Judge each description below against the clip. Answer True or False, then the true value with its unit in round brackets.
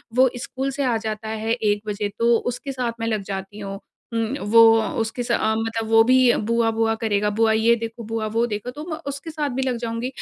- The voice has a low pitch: False (225 Hz)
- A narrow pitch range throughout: True (2.0 semitones)